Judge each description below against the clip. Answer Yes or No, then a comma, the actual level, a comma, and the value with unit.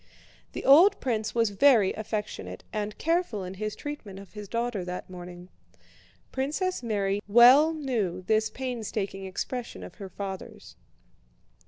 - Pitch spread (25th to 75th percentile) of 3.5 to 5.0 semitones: Yes, average, 4.7 semitones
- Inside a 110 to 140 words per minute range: Yes, slow, 135 wpm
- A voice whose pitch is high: Yes, high, 215 Hz